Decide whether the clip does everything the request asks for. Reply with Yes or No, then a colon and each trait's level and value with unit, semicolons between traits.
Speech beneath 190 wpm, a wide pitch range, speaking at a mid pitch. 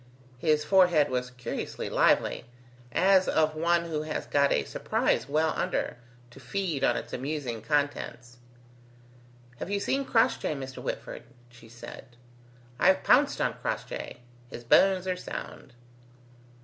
Yes: slow, 135 wpm; wide, 6.5 semitones; medium, 155 Hz